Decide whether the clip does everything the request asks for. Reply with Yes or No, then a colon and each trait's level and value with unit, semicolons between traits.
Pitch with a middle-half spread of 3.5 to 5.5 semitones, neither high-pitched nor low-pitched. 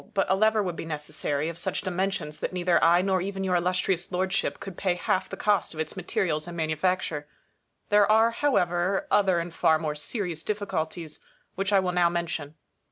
No: average, 2.9 semitones; medium, 180 Hz